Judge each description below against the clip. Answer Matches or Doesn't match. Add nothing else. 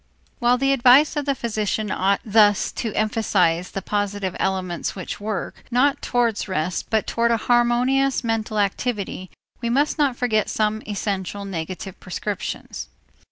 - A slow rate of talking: Doesn't match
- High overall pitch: Matches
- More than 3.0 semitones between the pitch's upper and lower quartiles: Matches